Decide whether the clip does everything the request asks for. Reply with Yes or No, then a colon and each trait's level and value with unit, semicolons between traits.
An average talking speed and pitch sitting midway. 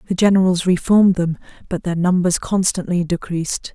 Yes: average, 145 wpm; medium, 180 Hz